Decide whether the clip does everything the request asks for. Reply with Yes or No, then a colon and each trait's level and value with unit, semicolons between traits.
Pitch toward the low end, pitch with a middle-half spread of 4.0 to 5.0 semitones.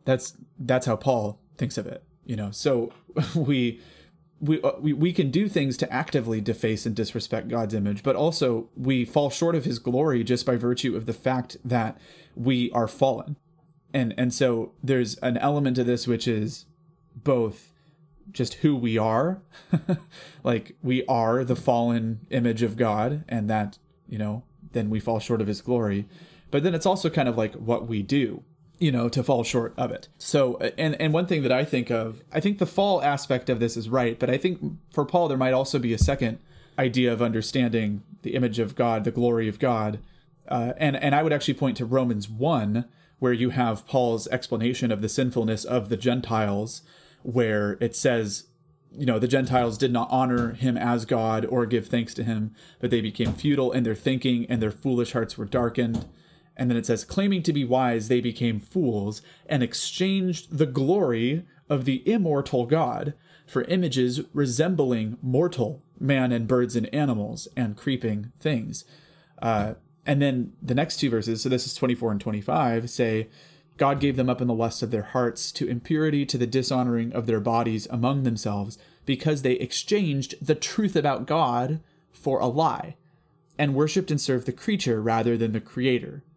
Yes: low, 125 Hz; average, 4.3 semitones